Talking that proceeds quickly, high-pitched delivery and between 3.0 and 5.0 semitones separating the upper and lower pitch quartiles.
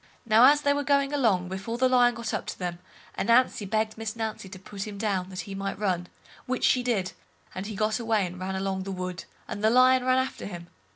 Yes: fast, 235 wpm; high, 215 Hz; average, 4.3 semitones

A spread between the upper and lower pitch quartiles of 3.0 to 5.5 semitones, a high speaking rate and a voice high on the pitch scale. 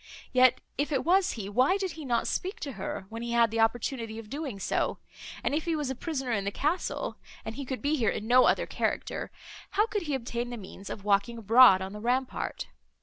Yes: average, 4.7 semitones; fast, 225 wpm; high, 245 Hz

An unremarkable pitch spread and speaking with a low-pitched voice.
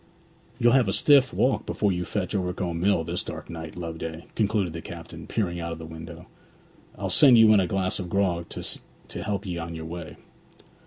Yes: average, 3.5 semitones; very low, 90 Hz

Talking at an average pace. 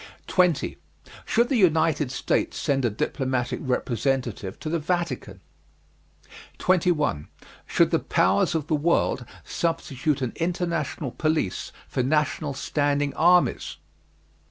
No: slow, 110 wpm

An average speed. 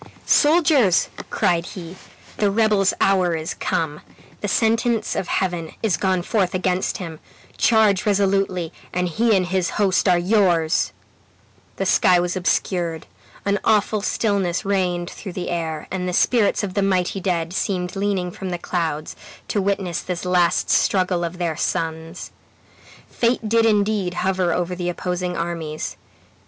Yes: average, 145 wpm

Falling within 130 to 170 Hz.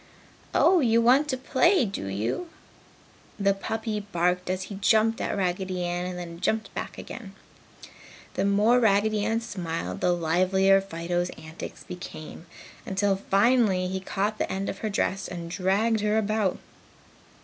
No: high, 195 Hz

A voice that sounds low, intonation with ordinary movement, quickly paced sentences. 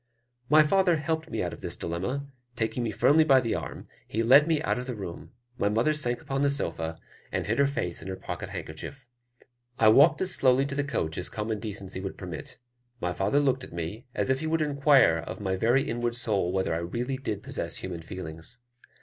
No: low, 120 Hz; wide, 6.9 semitones; fast, 220 wpm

